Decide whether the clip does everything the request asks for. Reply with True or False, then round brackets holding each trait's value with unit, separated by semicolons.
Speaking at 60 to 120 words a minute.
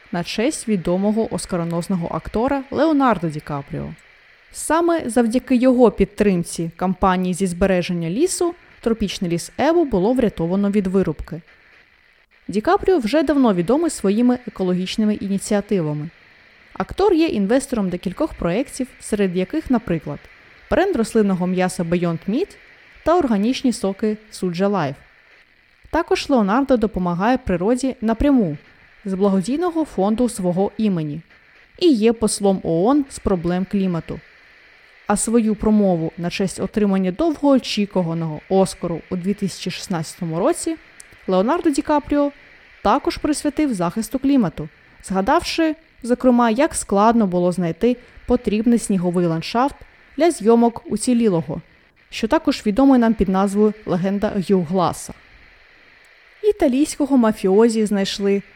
True (110 wpm)